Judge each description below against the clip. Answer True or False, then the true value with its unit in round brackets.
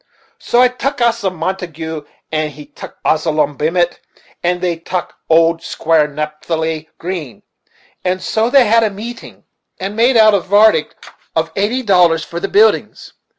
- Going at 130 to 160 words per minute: True (155 wpm)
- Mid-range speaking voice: True (175 Hz)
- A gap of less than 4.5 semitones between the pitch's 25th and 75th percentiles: False (5.2 semitones)